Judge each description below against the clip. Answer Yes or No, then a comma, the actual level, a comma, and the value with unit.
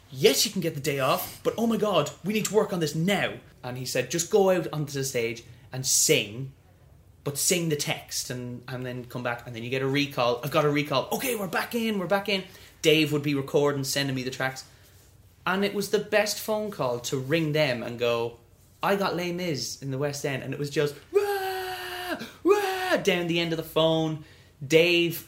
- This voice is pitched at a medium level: Yes, medium, 150 Hz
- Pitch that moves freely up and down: Yes, wide, 6.9 semitones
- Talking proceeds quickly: Yes, fast, 230 wpm